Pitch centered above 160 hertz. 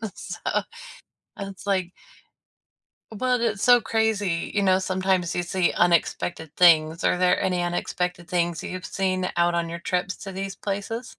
Yes: medium, 185 Hz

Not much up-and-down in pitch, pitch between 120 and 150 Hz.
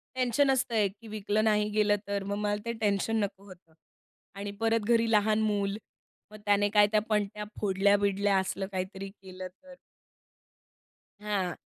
No: narrow, 1.5 semitones; high, 205 Hz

